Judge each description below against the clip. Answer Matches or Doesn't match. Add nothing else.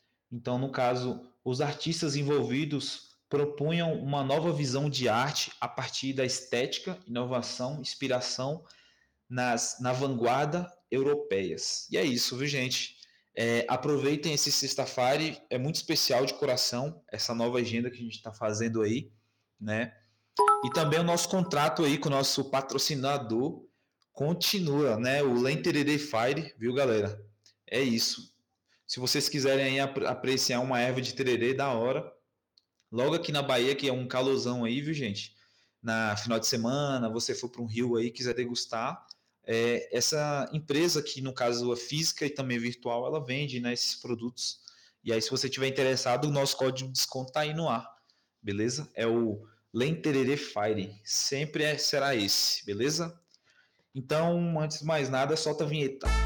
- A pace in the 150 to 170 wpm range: Matches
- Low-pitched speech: Matches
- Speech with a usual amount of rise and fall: Matches